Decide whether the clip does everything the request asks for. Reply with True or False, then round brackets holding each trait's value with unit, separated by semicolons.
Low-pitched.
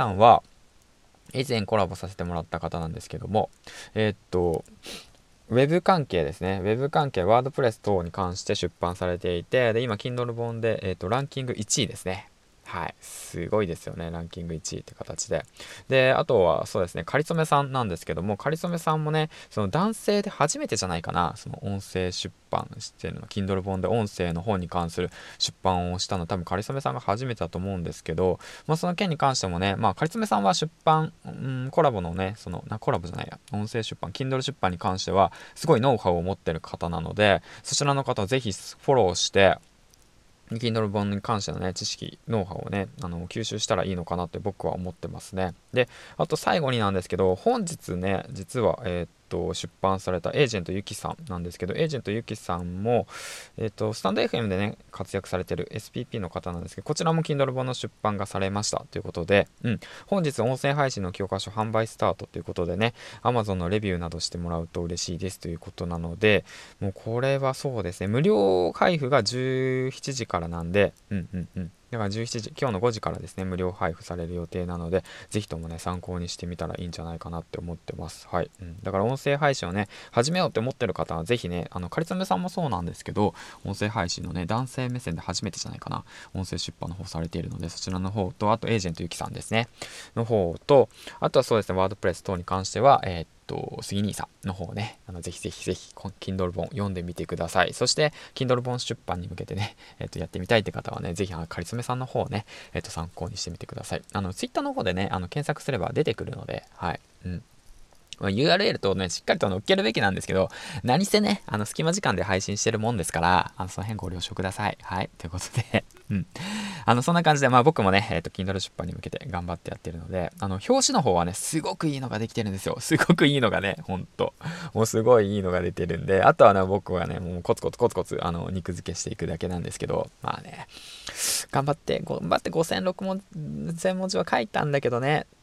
True (100 Hz)